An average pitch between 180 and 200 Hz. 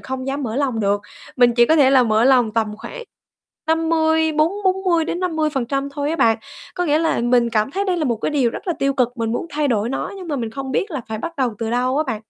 No: very high, 270 Hz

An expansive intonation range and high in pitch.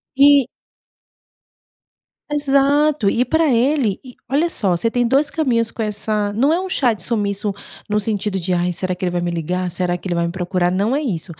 Yes: wide, 6.9 semitones; high, 215 Hz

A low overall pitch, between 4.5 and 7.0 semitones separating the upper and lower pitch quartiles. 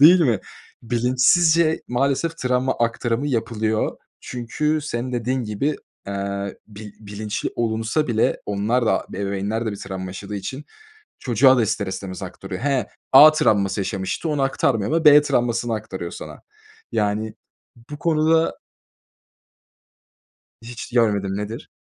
Yes: low, 115 Hz; average, 4.8 semitones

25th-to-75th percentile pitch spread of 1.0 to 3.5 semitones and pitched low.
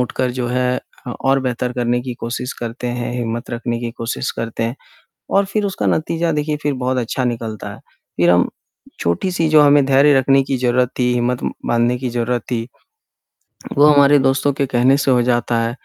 Yes: narrow, 2.5 semitones; low, 125 Hz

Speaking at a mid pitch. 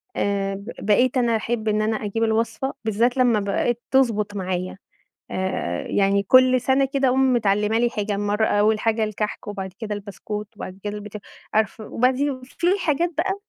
No: high, 215 Hz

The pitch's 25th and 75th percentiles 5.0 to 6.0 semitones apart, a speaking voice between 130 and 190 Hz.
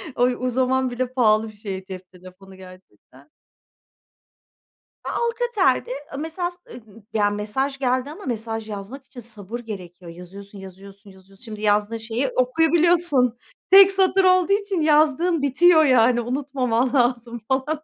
No: wide, 5.5 semitones; high, 245 Hz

